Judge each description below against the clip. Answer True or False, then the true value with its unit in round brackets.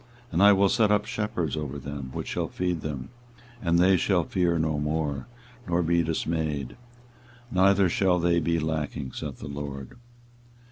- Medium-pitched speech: False (85 Hz)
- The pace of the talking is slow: False (170 wpm)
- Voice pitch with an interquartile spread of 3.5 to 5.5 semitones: True (3.8 semitones)